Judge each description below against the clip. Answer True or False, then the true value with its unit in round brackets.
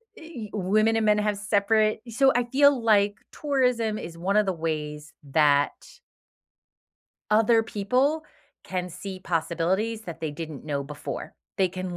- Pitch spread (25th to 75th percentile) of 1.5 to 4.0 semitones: False (5.2 semitones)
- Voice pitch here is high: True (205 Hz)